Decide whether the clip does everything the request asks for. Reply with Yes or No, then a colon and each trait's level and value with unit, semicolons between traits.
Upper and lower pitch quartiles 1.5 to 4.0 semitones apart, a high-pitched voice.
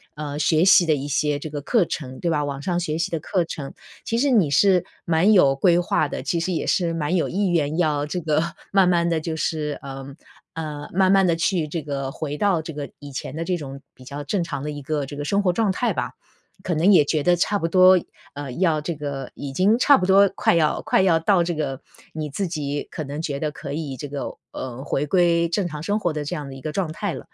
No: average, 3.6 semitones; medium, 160 Hz